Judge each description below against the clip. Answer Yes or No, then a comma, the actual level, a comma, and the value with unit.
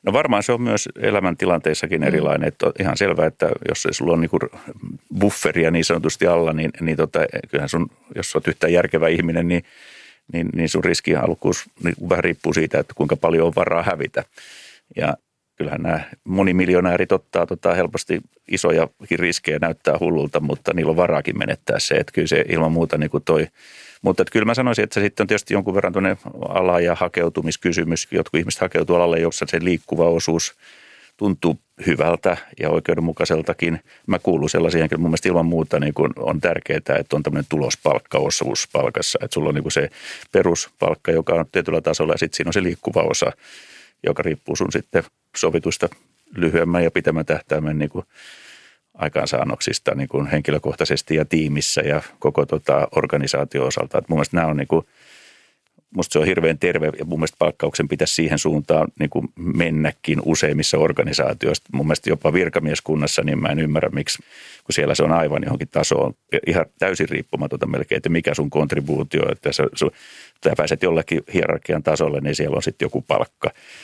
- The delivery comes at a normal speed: No, fast, 175 wpm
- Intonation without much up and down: Yes, narrow, 2.2 semitones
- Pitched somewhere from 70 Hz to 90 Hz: Yes, very low, 85 Hz